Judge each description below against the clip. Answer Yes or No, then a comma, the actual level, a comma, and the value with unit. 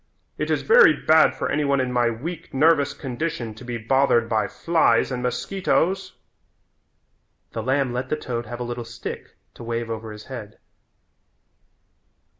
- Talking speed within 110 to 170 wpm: Yes, average, 160 wpm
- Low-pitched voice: Yes, low, 125 Hz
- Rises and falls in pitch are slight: No, average, 4.4 semitones